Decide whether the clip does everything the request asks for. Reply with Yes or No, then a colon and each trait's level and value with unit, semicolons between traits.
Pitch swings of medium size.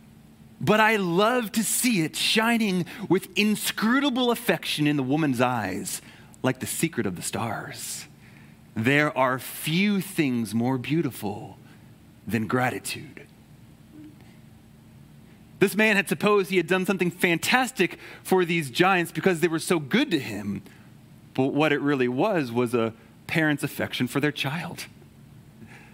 No: wide, 7.0 semitones